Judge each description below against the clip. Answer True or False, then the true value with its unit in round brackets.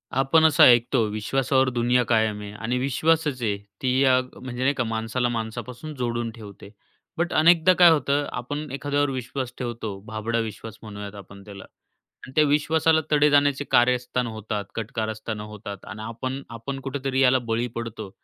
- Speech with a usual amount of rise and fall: True (3.8 semitones)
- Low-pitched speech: True (125 Hz)